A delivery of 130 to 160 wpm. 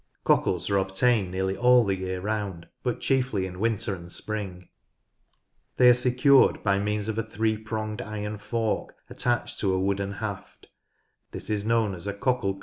No: average, 180 wpm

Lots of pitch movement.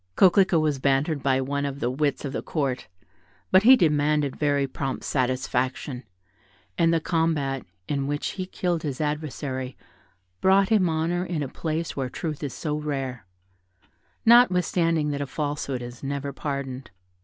No: average, 3.3 semitones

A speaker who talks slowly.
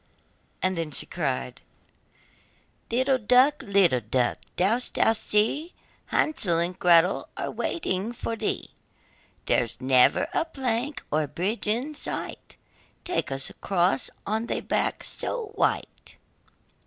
Yes: slow, 115 wpm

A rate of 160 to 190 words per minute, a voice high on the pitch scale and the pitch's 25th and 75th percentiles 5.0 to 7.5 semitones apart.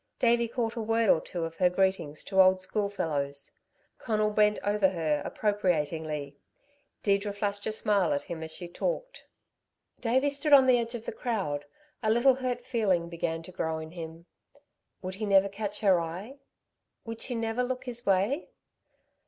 Yes: average, 170 wpm; high, 200 Hz; average, 5.3 semitones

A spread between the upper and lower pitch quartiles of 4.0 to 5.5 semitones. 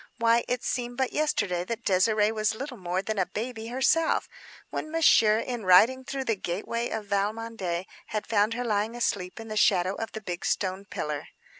No: average, 3.4 semitones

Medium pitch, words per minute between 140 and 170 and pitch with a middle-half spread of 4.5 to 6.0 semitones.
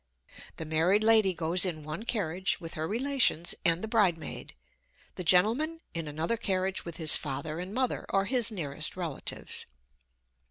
Yes: medium, 180 Hz; average, 155 wpm; average, 5.2 semitones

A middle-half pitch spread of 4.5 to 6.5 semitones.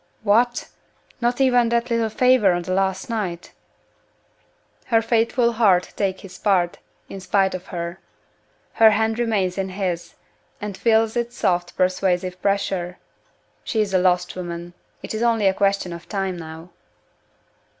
No: average, 3.8 semitones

